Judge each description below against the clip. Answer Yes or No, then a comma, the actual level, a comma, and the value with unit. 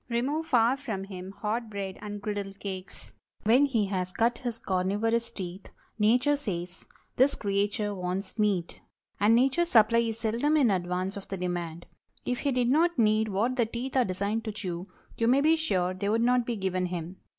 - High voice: Yes, high, 215 Hz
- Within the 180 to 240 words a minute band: Yes, average, 185 wpm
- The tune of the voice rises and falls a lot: No, average, 4.1 semitones